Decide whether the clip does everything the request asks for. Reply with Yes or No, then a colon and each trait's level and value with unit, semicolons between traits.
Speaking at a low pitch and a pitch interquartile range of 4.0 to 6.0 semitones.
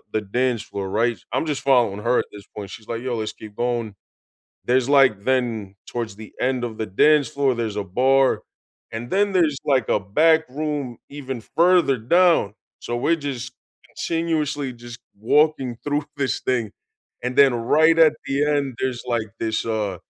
Yes: low, 130 Hz; average, 4.4 semitones